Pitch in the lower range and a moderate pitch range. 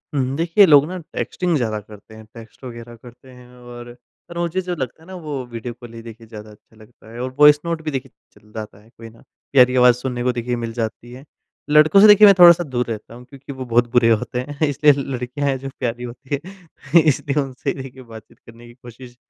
Yes: low, 125 Hz; average, 3.7 semitones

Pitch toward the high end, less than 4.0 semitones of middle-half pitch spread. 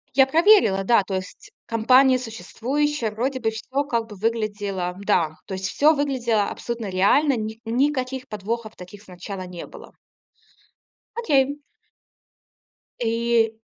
No: high, 230 Hz; average, 4.5 semitones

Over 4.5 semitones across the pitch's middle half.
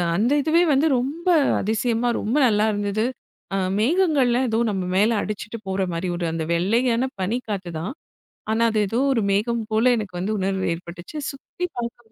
No: average, 4.1 semitones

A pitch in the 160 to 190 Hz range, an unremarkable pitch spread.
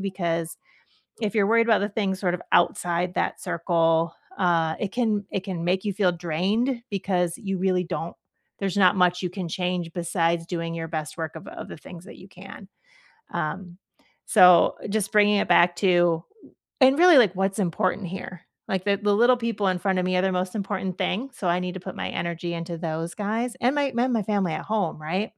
Yes: medium, 185 Hz; average, 3.0 semitones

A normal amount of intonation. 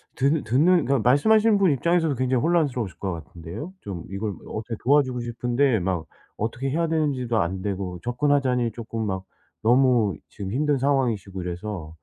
No: wide, 6.2 semitones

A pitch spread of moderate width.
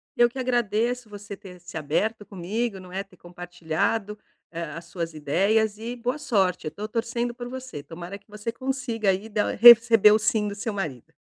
Yes: average, 4.4 semitones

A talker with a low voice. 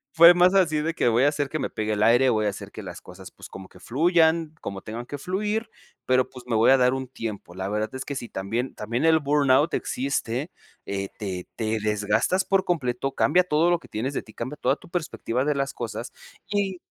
Yes: low, 130 Hz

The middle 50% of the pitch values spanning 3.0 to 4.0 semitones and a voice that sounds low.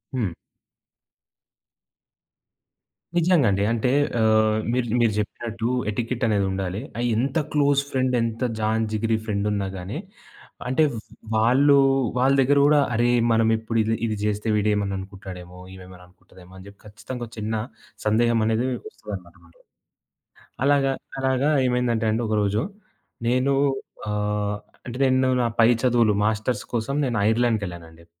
Yes: average, 3.4 semitones; low, 110 Hz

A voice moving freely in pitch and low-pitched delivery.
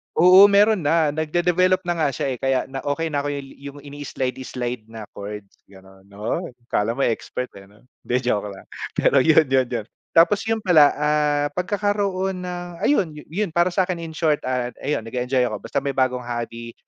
No: wide, 5.9 semitones; medium, 145 Hz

